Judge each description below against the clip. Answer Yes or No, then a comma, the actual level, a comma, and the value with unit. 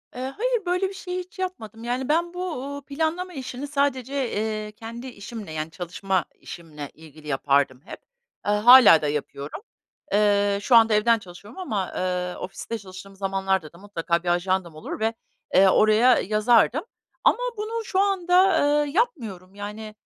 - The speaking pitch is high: Yes, high, 215 Hz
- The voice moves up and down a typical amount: No, wide, 7.3 semitones